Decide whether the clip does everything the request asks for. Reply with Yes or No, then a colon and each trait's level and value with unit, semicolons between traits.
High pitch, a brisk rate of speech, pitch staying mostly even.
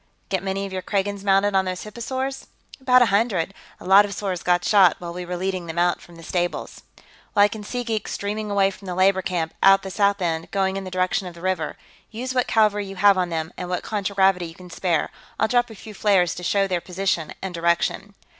Yes: high, 195 Hz; fast, 240 wpm; narrow, 2.3 semitones